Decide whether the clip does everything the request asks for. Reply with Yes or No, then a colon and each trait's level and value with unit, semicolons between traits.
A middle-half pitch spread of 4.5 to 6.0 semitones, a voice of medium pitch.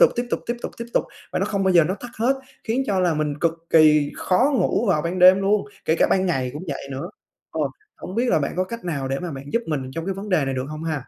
Yes: average, 4.9 semitones; medium, 175 Hz